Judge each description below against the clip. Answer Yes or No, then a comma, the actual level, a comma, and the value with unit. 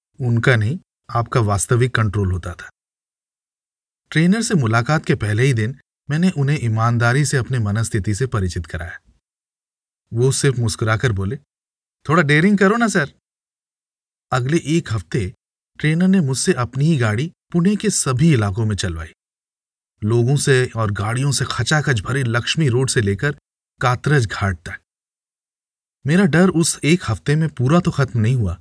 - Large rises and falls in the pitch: Yes, wide, 5.7 semitones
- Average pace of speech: Yes, average, 150 wpm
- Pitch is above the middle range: No, low, 130 Hz